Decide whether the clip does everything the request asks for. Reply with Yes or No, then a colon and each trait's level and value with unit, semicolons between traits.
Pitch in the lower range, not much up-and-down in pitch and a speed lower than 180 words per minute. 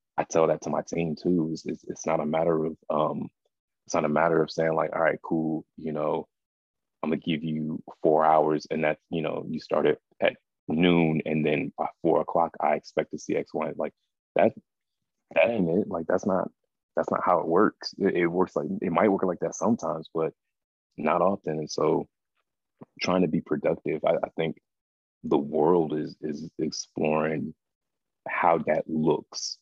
No: very low, 80 Hz; narrow, 1.0 semitones; average, 190 wpm